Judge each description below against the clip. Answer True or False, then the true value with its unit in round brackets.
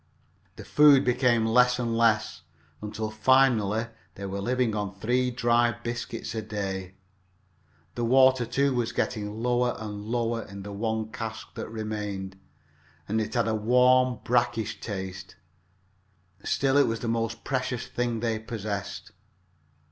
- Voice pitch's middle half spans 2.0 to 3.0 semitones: True (2.5 semitones)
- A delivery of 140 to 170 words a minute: True (145 wpm)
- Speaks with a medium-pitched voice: False (115 Hz)